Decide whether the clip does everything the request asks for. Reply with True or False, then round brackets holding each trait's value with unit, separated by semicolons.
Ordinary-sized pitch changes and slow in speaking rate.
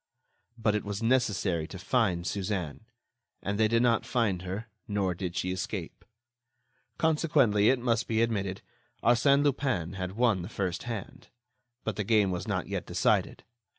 False (3.9 semitones; 155 wpm)